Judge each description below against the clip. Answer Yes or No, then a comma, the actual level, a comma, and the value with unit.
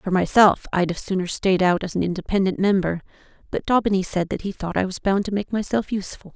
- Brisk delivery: Yes, fast, 225 wpm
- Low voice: No, high, 190 Hz